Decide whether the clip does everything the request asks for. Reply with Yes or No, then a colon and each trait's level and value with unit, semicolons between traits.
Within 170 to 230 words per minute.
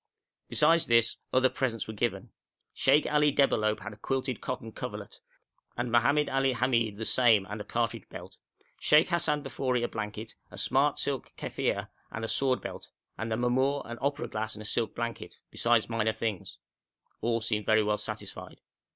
Yes: average, 175 wpm